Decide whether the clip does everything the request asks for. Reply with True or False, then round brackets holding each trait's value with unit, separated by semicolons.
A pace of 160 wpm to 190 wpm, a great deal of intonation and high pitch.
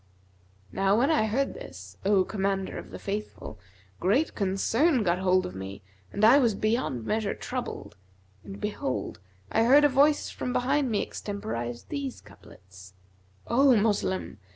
False (150 wpm; 6.3 semitones; 205 Hz)